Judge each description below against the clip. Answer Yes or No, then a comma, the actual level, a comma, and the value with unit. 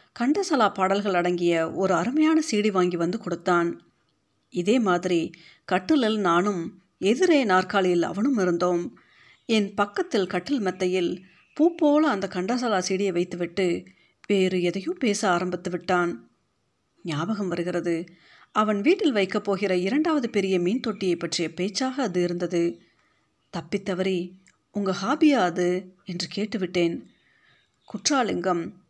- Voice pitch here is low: No, medium, 185 Hz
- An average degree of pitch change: Yes, average, 3.4 semitones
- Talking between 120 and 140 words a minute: No, average, 110 wpm